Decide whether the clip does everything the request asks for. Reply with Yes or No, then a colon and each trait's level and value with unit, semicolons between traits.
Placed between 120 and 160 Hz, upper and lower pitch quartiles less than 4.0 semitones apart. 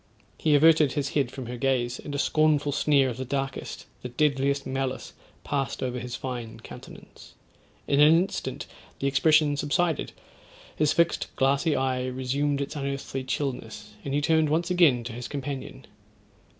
Yes: medium, 140 Hz; narrow, 2.4 semitones